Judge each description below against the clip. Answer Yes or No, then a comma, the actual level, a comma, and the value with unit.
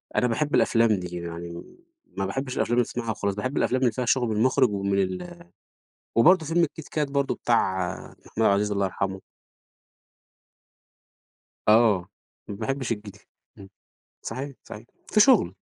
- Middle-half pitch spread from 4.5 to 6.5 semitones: Yes, average, 5.3 semitones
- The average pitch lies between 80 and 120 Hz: Yes, low, 115 Hz